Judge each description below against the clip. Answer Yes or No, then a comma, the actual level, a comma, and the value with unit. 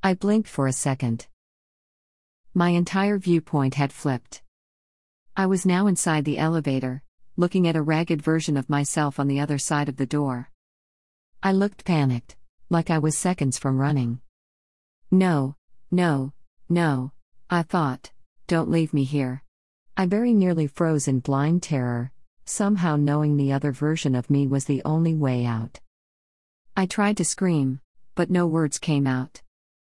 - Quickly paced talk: No, average, 155 wpm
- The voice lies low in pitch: No, medium, 145 Hz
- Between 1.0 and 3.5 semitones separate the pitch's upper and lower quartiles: No, average, 4.7 semitones